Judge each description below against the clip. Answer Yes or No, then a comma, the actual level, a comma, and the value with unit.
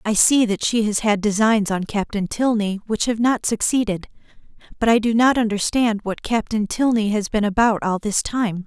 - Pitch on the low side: No, high, 215 Hz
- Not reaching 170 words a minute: No, average, 195 wpm